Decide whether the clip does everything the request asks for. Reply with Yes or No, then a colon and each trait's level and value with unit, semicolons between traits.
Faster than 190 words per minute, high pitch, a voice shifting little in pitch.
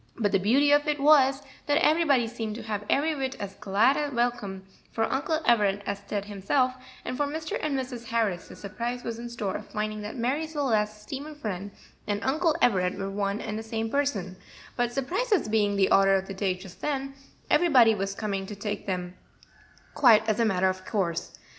No: average, 200 wpm; high, 225 Hz; average, 5.3 semitones